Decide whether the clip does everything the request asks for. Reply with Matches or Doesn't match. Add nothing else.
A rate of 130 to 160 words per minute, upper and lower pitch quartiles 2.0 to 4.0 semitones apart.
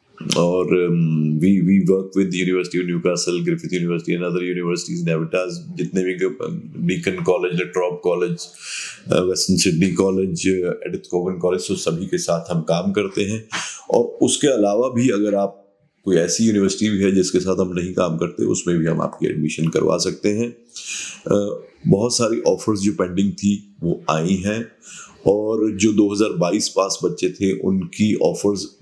Matches